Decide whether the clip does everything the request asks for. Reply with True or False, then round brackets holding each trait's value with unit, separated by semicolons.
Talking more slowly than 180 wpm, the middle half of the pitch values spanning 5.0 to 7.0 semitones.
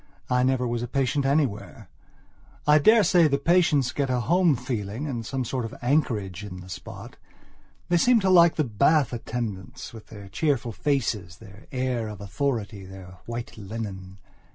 True (165 wpm; 5.6 semitones)